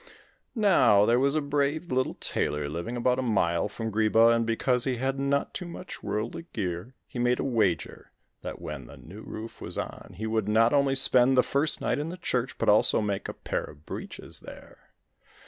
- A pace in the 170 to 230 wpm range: Yes, average, 200 wpm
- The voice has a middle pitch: No, low, 120 Hz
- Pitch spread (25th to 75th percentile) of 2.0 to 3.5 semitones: No, average, 4.3 semitones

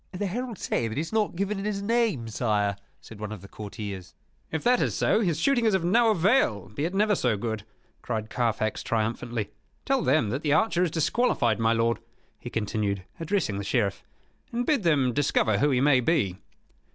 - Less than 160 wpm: No, average, 200 wpm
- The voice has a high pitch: No, low, 135 Hz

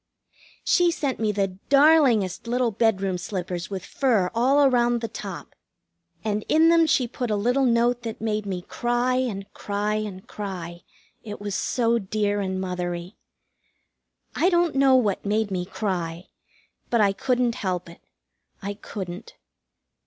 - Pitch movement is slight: No, average, 4.5 semitones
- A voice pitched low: No, high, 215 Hz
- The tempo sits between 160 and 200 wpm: No, average, 150 wpm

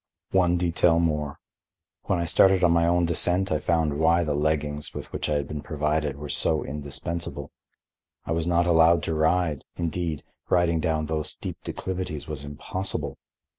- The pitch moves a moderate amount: No, narrow, 2.3 semitones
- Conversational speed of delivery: Yes, average, 170 wpm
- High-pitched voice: No, very low, 80 Hz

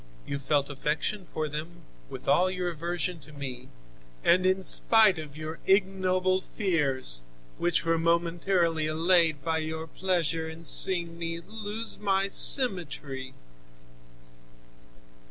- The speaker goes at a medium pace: No, slow, 120 wpm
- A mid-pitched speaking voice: Yes, medium, 170 Hz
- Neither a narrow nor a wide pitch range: Yes, average, 3.2 semitones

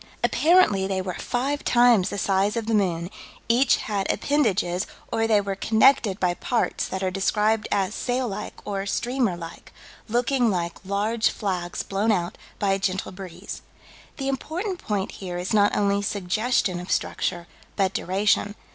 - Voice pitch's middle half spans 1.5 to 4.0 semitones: Yes, average, 3.6 semitones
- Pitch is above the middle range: Yes, high, 200 Hz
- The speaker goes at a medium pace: Yes, average, 160 wpm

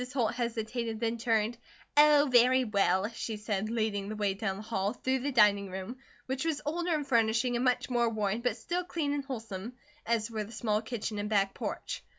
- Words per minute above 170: Yes, average, 200 wpm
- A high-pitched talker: Yes, high, 230 Hz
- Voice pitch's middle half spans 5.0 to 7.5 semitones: No, average, 3.2 semitones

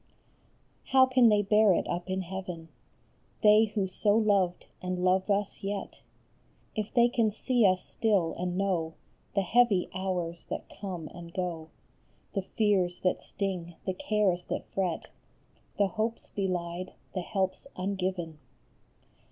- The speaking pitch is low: No, high, 190 Hz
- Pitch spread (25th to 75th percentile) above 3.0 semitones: No, average, 2.7 semitones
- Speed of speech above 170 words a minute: No, average, 140 wpm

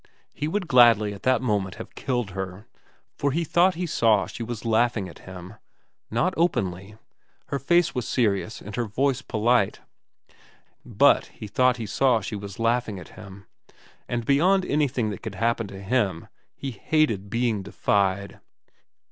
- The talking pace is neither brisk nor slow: Yes, average, 160 wpm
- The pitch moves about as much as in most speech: Yes, average, 4.5 semitones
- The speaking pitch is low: Yes, low, 115 Hz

